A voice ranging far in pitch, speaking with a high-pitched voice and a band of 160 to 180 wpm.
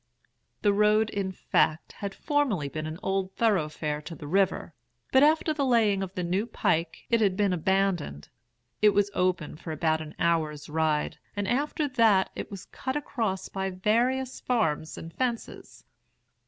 Yes: wide, 5.7 semitones; high, 195 Hz; average, 165 wpm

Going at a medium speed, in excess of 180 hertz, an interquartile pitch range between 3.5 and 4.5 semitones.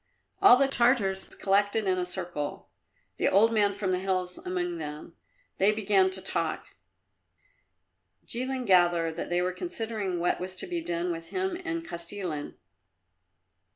Yes: average, 150 wpm; high, 190 Hz; average, 4.1 semitones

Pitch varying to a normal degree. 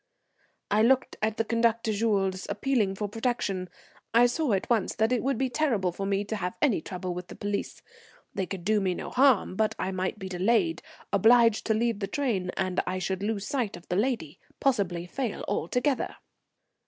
Yes: average, 3.9 semitones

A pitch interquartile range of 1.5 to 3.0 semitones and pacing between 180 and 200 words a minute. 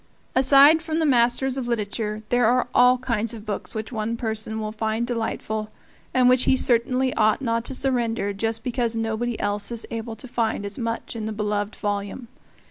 Yes: narrow, 2.4 semitones; average, 190 wpm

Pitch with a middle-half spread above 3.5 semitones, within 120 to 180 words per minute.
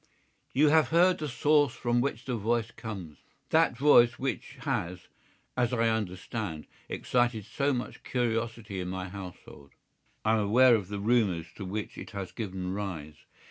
Yes: average, 4.5 semitones; average, 155 wpm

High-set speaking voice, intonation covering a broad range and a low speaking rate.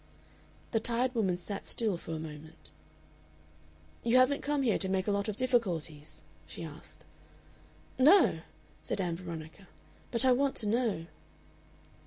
No: high, 200 Hz; wide, 6.9 semitones; average, 145 wpm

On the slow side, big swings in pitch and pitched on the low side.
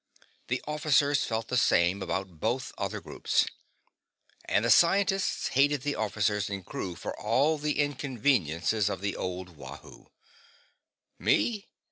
Yes: slow, 130 wpm; wide, 7.0 semitones; low, 120 Hz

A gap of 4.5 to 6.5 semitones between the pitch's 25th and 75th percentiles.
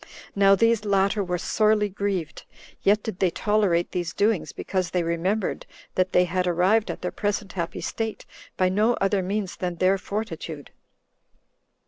No: average, 2.7 semitones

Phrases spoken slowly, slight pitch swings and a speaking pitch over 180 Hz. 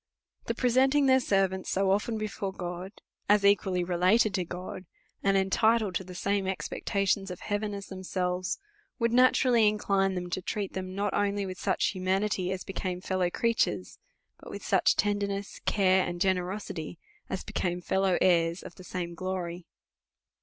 No: average, 160 wpm; narrow, 2.0 semitones; high, 190 Hz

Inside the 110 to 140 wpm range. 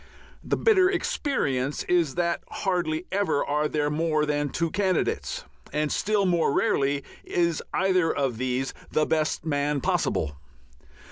Yes: slow, 135 wpm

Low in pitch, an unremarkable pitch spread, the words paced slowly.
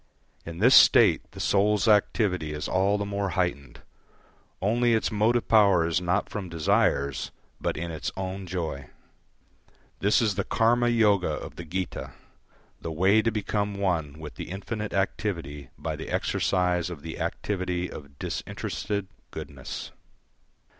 No: very low, 95 Hz; average, 4.0 semitones; average, 145 wpm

